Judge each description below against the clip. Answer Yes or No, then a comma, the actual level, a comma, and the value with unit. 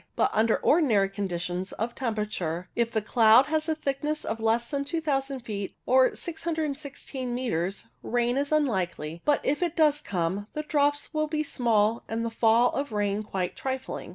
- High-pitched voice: Yes, high, 240 Hz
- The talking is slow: No, average, 165 wpm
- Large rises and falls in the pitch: Yes, wide, 5.8 semitones